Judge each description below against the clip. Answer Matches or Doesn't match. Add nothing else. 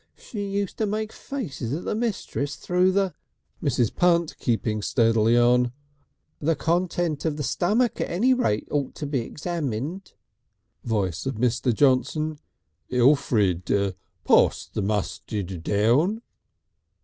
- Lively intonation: Matches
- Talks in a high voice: Doesn't match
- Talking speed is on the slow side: Matches